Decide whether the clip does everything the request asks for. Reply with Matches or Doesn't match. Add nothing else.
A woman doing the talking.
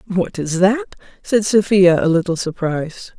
Matches